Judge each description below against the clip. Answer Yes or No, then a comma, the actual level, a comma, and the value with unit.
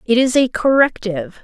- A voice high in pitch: Yes, high, 235 Hz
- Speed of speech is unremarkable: Yes, average, 165 wpm